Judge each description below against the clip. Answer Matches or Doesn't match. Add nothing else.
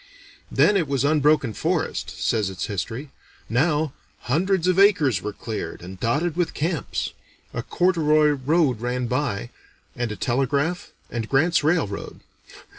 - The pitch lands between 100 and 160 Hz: Matches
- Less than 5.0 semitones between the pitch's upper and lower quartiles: Doesn't match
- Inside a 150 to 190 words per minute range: Doesn't match